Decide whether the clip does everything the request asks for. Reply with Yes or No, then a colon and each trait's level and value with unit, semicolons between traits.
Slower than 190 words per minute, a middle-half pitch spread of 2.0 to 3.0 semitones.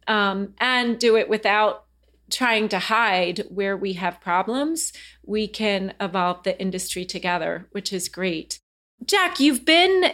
No: average, 140 wpm; average, 4.0 semitones